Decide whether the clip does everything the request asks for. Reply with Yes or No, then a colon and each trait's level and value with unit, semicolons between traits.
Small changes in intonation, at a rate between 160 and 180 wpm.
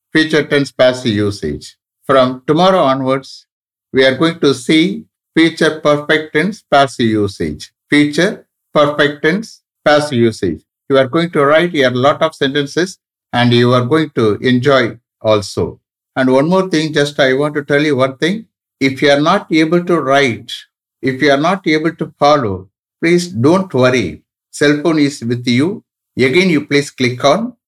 No: average, 3.8 semitones; average, 165 wpm